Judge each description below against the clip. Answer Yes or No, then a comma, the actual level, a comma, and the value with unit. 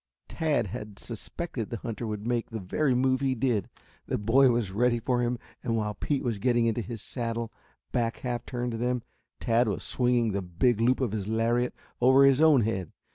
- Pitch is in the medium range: No, low, 120 Hz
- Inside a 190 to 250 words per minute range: Yes, average, 200 wpm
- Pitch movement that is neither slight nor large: No, narrow, 2.1 semitones